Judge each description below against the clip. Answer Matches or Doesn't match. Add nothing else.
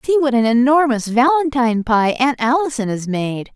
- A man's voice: Doesn't match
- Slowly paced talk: Doesn't match